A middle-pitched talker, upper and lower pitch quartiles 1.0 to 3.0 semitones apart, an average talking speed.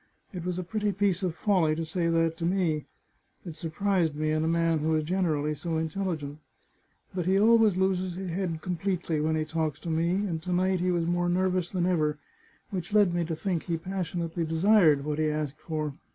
No: medium, 170 Hz; average, 2.7 semitones; fast, 210 wpm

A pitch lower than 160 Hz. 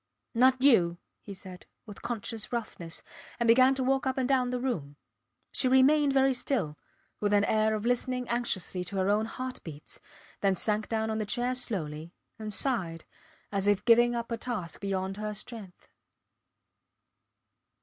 No: high, 220 Hz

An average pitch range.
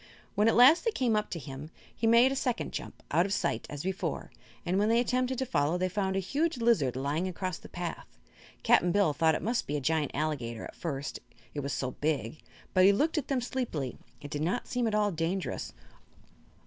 No: wide, 7.6 semitones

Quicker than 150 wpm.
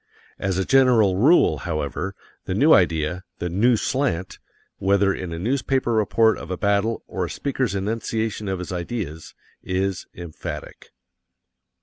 No: average, 140 wpm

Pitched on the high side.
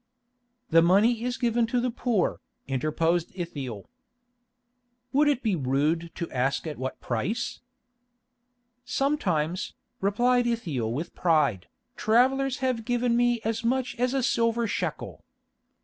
Yes: high, 220 Hz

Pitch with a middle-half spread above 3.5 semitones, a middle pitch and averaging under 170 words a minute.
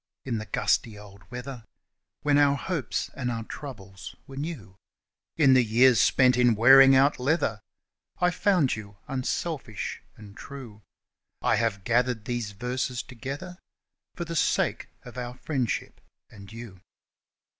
No: average, 4.0 semitones; low, 125 Hz; average, 140 wpm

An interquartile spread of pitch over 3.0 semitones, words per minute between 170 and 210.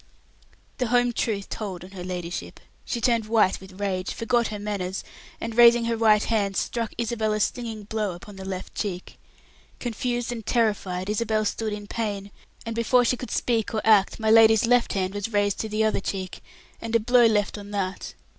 No: narrow, 2.6 semitones; average, 195 wpm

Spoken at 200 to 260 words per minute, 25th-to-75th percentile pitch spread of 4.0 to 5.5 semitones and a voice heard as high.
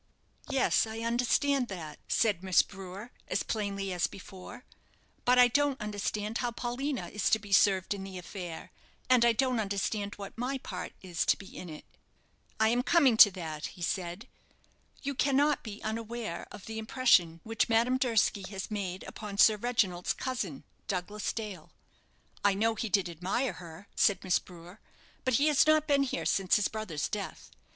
No: average, 175 wpm; average, 4.4 semitones; high, 210 Hz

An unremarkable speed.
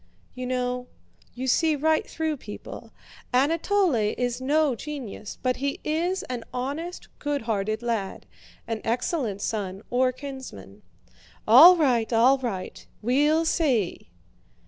No: slow, 120 wpm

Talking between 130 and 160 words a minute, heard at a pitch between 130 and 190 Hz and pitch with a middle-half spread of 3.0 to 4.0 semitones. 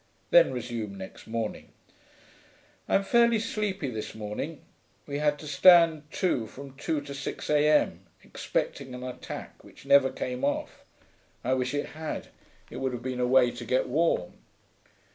Yes: average, 155 wpm; medium, 140 Hz; average, 3.5 semitones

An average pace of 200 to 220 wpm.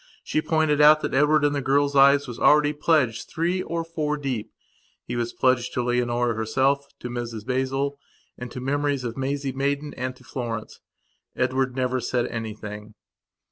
No: average, 175 wpm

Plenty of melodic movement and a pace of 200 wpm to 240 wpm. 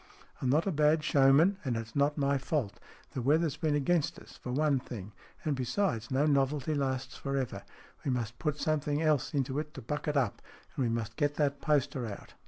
No: average, 2.8 semitones; fast, 205 wpm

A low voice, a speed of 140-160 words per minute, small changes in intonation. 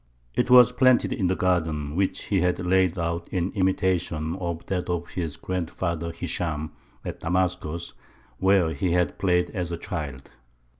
Yes: very low, 90 Hz; average, 155 wpm; narrow, 2.1 semitones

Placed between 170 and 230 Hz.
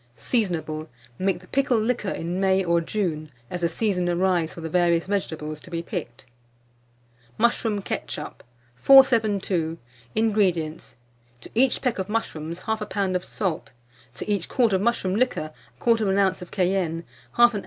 Yes: high, 190 Hz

